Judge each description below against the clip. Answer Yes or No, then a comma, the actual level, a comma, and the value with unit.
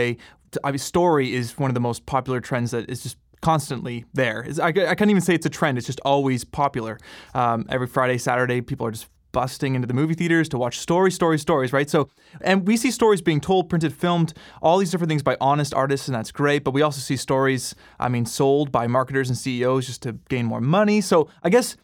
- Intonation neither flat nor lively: Yes, average, 4.6 semitones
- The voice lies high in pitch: No, low, 135 Hz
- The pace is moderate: No, fast, 225 wpm